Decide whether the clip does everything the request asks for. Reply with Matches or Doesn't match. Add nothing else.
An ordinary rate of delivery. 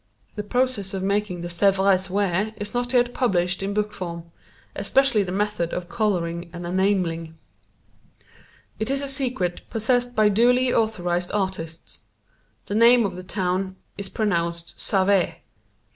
Matches